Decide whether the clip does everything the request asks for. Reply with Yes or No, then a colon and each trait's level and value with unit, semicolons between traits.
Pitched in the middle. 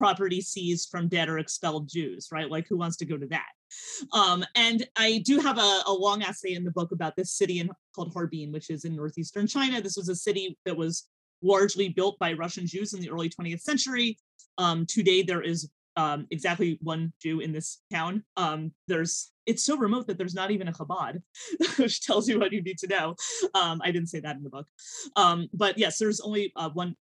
Yes: medium, 180 Hz